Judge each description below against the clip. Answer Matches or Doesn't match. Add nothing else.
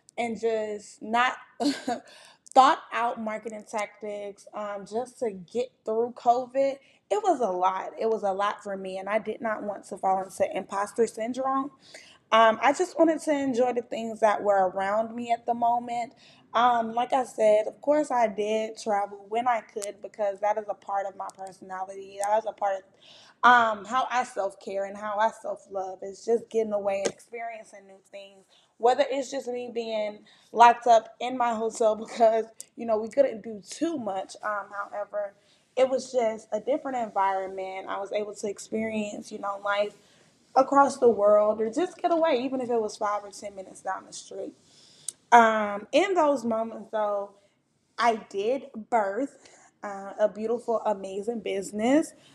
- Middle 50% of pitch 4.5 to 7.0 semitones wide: Doesn't match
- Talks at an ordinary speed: Matches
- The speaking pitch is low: Doesn't match